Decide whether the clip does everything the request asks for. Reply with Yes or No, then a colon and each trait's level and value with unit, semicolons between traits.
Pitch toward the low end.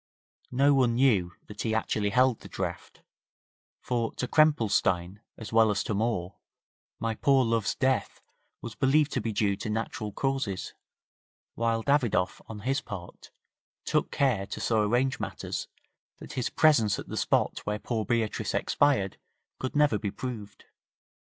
Yes: low, 115 Hz